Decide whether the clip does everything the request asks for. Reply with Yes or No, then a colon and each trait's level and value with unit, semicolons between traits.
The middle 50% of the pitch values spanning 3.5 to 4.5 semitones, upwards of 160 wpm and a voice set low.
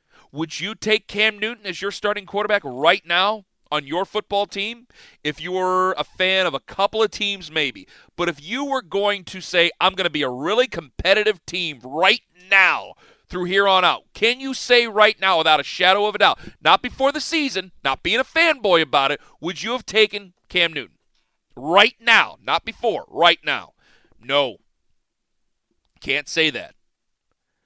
No: average, 4.0 semitones; average, 180 wpm; high, 195 Hz